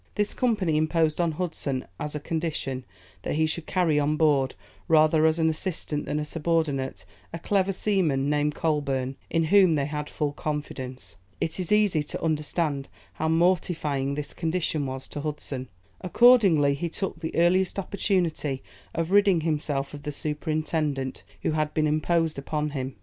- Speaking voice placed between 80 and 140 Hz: No, medium, 155 Hz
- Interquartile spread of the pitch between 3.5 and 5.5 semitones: No, narrow, 2.5 semitones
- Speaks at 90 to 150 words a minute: No, average, 165 wpm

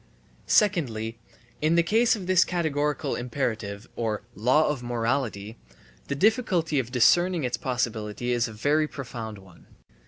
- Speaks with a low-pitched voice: Yes, low, 125 Hz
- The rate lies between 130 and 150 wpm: Yes, slow, 135 wpm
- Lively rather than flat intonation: Yes, wide, 5.8 semitones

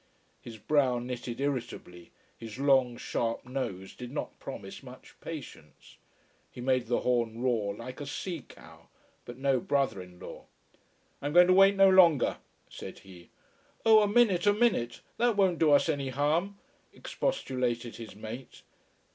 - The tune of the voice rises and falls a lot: Yes, wide, 6.3 semitones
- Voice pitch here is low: Yes, low, 130 Hz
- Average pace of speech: Yes, average, 155 wpm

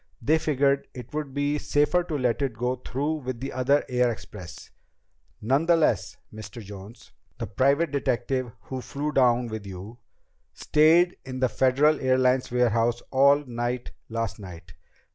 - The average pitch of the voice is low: Yes, low, 130 Hz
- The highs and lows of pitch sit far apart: No, average, 3.4 semitones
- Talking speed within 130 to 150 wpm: Yes, average, 145 wpm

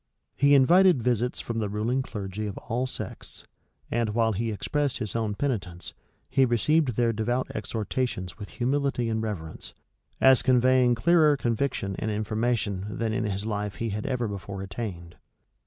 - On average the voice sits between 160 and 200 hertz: No, low, 115 Hz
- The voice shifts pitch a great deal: No, average, 3.6 semitones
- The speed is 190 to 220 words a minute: No, average, 155 wpm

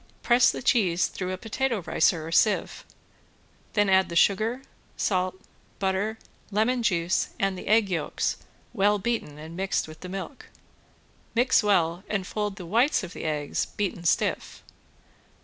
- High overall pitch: Yes, high, 195 Hz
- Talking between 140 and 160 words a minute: Yes, average, 150 wpm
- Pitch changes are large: No, average, 3.7 semitones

